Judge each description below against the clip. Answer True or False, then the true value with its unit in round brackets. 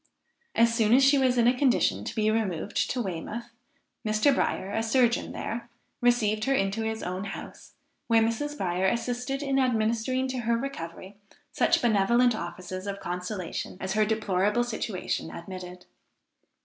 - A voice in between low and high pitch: False (220 Hz)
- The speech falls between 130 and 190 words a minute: True (155 wpm)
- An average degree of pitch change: True (4.2 semitones)